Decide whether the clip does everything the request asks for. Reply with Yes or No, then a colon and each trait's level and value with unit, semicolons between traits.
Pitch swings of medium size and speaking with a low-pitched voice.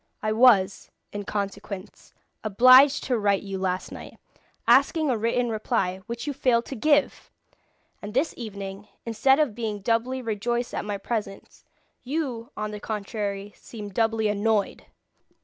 No: average, 3.3 semitones; high, 220 Hz